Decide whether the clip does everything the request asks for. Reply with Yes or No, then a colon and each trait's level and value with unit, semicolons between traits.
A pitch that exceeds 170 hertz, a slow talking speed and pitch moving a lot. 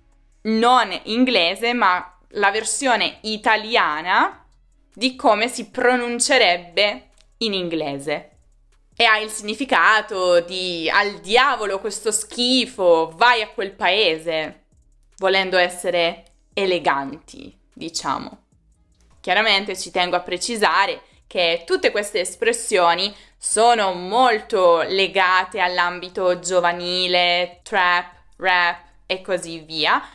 No: high, 190 Hz; slow, 95 wpm; average, 4.3 semitones